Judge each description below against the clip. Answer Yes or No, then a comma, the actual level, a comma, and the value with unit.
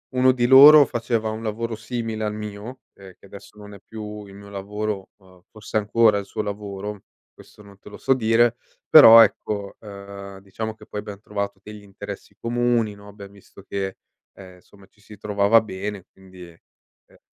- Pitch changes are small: Yes, narrow, 2.1 semitones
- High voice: No, low, 105 Hz